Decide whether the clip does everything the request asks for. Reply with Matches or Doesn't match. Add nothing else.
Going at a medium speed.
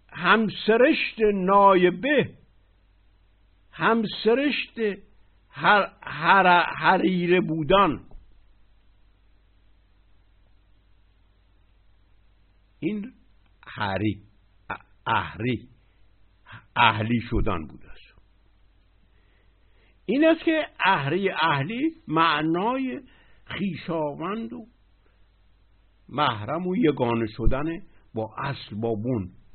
Doesn't match